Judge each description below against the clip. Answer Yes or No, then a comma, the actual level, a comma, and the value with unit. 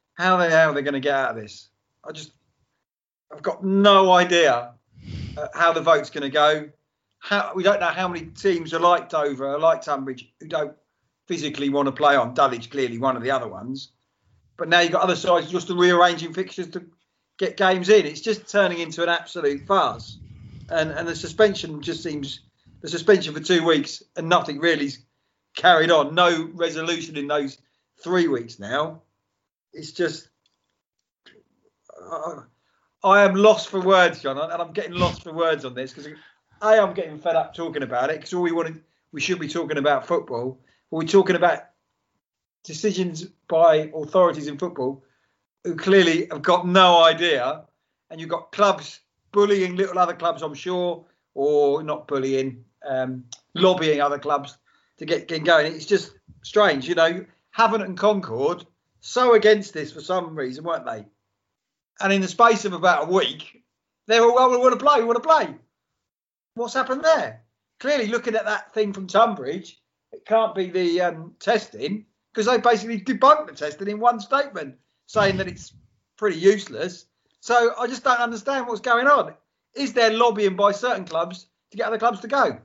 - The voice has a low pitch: No, medium, 170 Hz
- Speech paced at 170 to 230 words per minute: Yes, average, 180 wpm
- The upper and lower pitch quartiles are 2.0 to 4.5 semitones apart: No, wide, 5.4 semitones